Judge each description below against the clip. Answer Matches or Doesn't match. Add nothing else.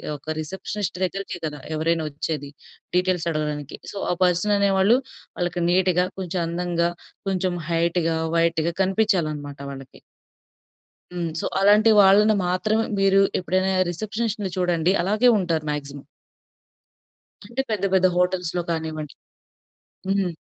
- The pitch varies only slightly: Doesn't match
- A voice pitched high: Doesn't match